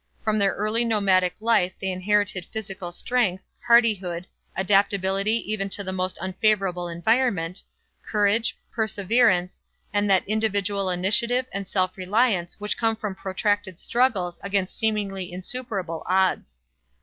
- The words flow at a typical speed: No, slow, 125 wpm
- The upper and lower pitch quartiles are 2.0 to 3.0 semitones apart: Yes, average, 2.7 semitones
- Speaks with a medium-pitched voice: No, high, 195 Hz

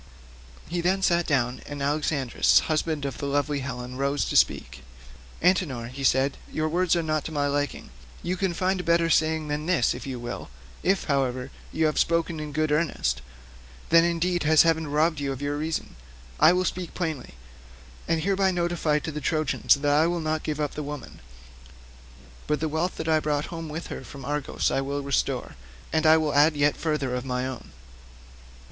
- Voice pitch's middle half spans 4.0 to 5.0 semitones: No, average, 2.8 semitones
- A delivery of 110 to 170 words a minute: No, average, 190 wpm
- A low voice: No, medium, 155 Hz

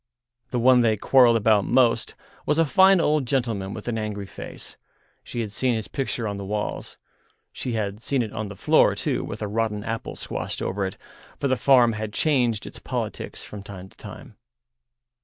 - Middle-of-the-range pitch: No, low, 115 Hz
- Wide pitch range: No, average, 3.7 semitones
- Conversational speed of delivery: Yes, average, 190 wpm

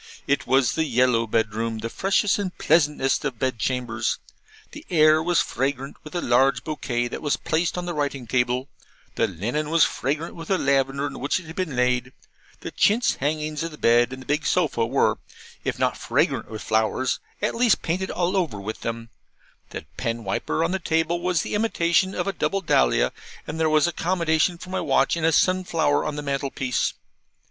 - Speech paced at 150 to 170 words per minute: No, average, 195 wpm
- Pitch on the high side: No, medium, 150 Hz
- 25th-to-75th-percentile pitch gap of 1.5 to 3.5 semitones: No, average, 5.2 semitones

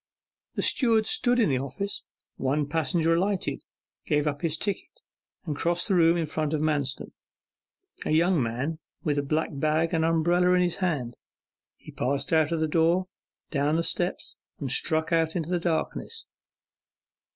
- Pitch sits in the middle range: Yes, medium, 160 Hz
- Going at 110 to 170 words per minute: Yes, average, 165 wpm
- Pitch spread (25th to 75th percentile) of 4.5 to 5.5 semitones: No, average, 2.9 semitones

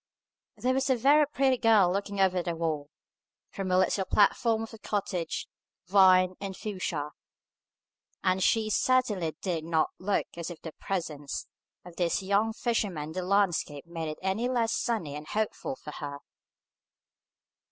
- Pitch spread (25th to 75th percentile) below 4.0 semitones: No, average, 4.6 semitones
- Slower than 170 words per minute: Yes, average, 155 wpm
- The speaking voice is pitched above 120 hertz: Yes, high, 190 Hz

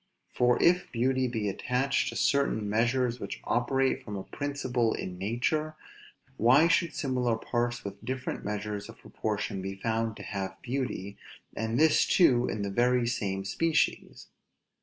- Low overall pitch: Yes, low, 120 Hz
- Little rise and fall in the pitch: No, average, 4.0 semitones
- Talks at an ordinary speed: Yes, average, 150 wpm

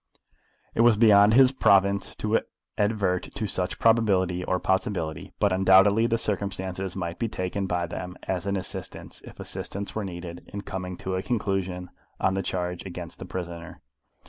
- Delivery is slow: No, average, 165 wpm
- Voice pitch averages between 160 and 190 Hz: No, very low, 95 Hz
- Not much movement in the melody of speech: Yes, narrow, 2.1 semitones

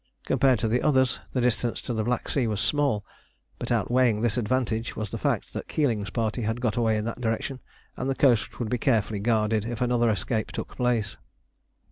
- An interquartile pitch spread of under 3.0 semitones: Yes, narrow, 2.4 semitones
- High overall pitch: No, low, 115 Hz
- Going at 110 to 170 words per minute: No, average, 200 wpm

